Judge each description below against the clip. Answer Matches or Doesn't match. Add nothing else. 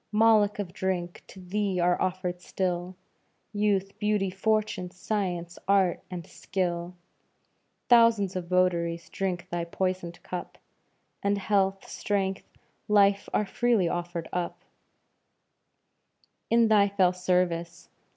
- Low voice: Doesn't match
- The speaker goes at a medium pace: Doesn't match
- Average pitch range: Doesn't match